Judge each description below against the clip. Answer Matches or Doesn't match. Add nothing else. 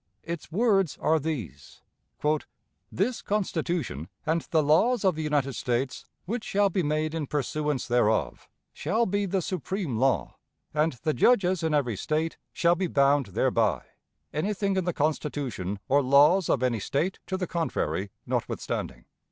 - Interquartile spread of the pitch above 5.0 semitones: Matches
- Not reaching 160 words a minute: Matches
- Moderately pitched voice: Matches